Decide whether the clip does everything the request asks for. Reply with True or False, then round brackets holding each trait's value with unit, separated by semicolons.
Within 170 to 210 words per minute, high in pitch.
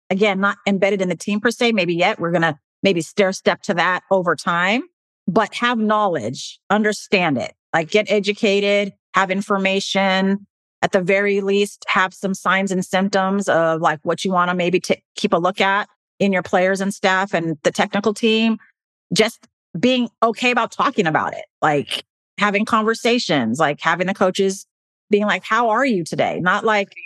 True (180 wpm; 195 Hz)